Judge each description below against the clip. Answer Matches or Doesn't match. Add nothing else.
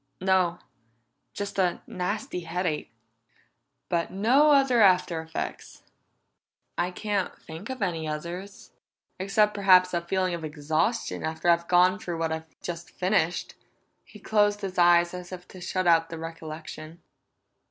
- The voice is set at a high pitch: Doesn't match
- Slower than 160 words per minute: Matches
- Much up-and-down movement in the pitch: Doesn't match